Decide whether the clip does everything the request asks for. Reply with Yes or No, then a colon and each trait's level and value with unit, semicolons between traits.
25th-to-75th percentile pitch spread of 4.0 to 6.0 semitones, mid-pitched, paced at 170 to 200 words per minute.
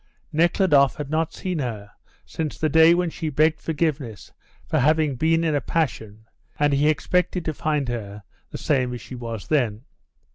Yes: average, 4.6 semitones; medium, 150 Hz; average, 175 wpm